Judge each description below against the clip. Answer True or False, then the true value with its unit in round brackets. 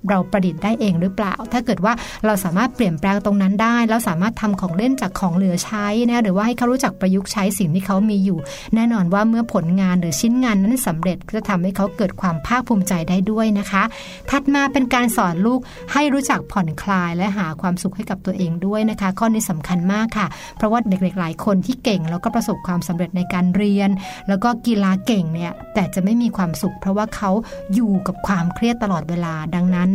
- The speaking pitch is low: False (200 Hz)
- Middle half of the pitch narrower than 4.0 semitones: True (3.4 semitones)